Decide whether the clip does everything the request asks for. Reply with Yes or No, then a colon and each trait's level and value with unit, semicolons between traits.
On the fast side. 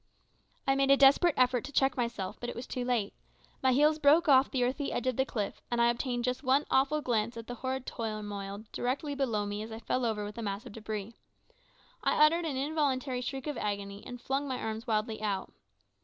Yes: fast, 220 wpm